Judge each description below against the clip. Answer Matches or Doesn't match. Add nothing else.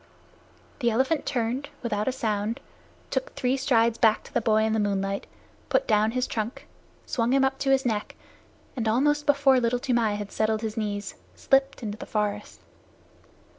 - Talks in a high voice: Matches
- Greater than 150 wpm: Matches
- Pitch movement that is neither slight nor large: Matches